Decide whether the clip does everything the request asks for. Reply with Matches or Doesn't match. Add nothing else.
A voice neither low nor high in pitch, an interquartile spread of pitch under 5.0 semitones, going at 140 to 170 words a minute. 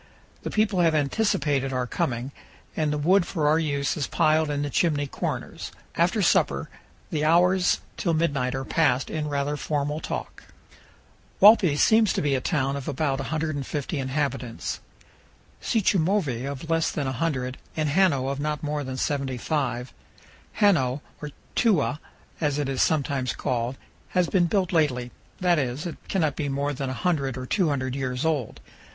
Matches